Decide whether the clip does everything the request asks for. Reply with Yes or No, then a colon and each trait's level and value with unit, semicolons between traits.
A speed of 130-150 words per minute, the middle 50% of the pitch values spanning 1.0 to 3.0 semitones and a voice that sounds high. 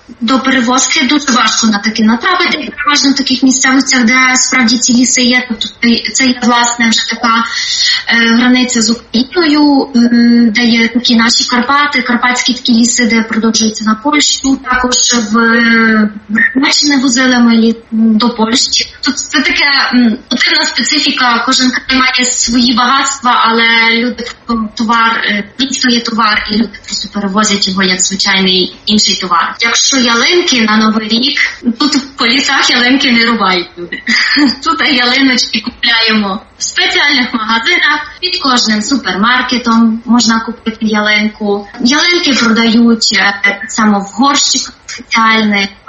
Yes: average, 135 wpm; average, 2.7 semitones; high, 240 Hz